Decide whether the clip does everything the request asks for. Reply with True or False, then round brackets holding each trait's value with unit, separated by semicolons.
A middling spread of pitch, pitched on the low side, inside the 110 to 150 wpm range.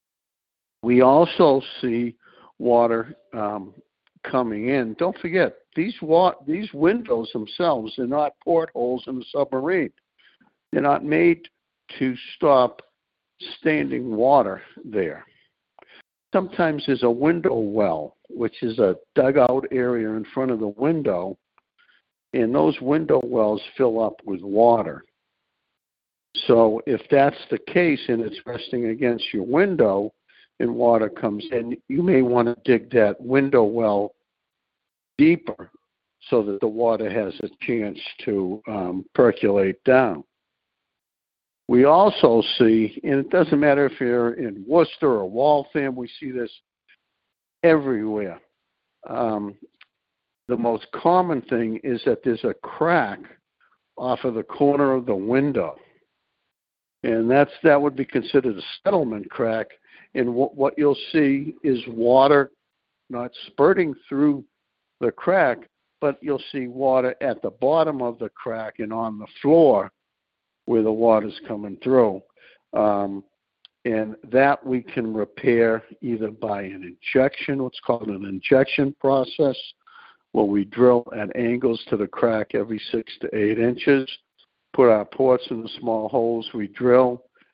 True (4.0 semitones; 125 Hz; 135 wpm)